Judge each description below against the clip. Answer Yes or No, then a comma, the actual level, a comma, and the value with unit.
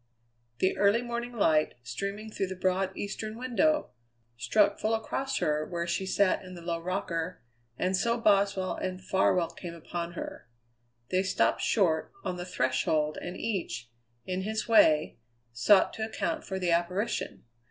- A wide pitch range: No, average, 3.8 semitones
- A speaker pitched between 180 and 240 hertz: Yes, medium, 185 Hz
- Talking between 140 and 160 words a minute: Yes, average, 155 wpm